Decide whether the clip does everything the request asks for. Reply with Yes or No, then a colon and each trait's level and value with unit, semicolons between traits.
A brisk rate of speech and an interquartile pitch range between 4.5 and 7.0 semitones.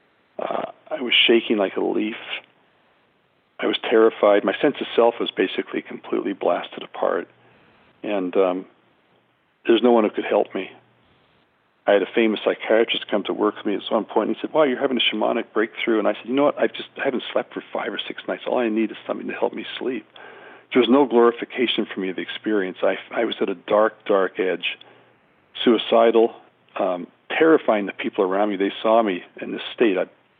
No: fast, 215 wpm; average, 2.9 semitones